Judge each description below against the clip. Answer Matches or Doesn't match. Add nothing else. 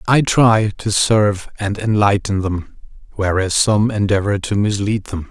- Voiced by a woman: Doesn't match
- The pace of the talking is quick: Doesn't match